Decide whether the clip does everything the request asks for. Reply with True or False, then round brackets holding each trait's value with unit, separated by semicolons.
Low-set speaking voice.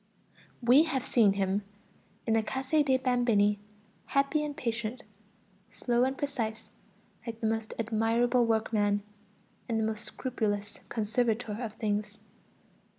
False (225 Hz)